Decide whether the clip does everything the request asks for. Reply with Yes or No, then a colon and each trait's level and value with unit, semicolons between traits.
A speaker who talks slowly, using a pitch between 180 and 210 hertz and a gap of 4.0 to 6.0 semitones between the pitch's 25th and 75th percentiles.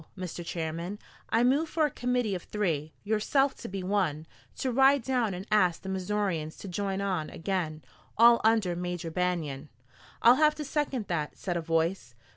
No: average, 175 wpm; high, 190 Hz; wide, 5.6 semitones